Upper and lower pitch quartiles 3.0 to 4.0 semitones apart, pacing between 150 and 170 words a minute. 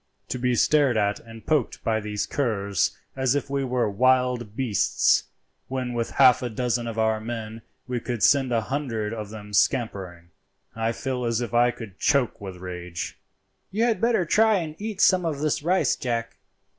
No: average, 3.7 semitones; average, 180 wpm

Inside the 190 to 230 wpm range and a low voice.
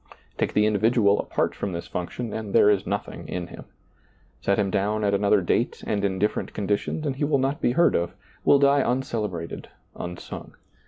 Yes: average, 195 wpm; low, 105 Hz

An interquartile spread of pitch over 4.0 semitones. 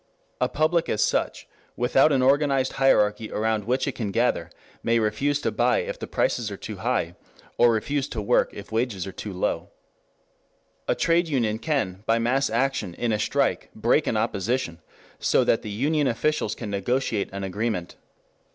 Yes: average, 4.5 semitones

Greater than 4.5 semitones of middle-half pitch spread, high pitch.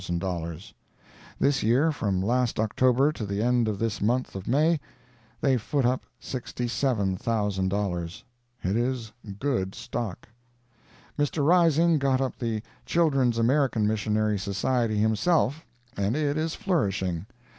No: average, 5.0 semitones; low, 120 Hz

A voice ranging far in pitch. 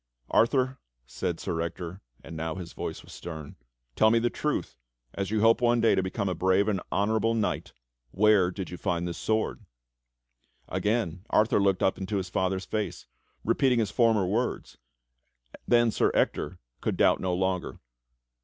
No: average, 3.7 semitones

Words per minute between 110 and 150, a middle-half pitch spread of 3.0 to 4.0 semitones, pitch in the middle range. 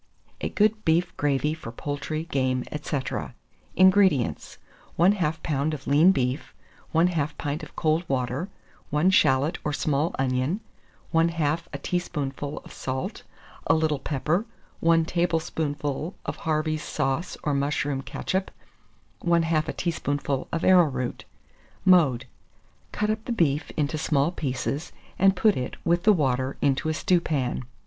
Yes: slow, 135 wpm; average, 3.6 semitones; medium, 155 Hz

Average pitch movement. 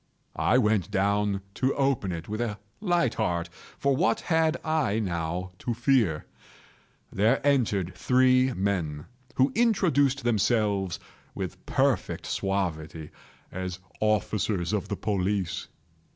No: wide, 5.8 semitones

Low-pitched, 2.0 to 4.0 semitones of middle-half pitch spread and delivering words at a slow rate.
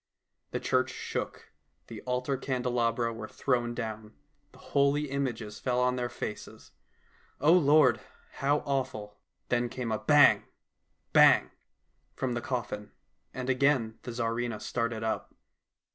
Yes: low, 125 Hz; average, 2.7 semitones; slow, 130 wpm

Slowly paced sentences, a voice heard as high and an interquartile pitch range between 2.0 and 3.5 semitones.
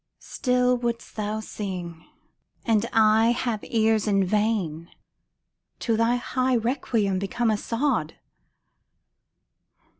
Yes: slow, 110 wpm; high, 220 Hz; average, 2.7 semitones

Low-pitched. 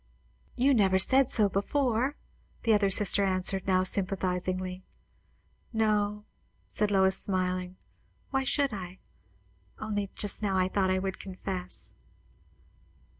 No: high, 195 Hz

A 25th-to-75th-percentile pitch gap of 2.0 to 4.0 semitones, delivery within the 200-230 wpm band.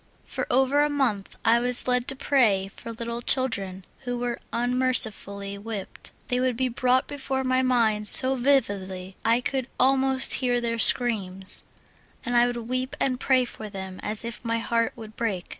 No: average, 3.1 semitones; average, 175 wpm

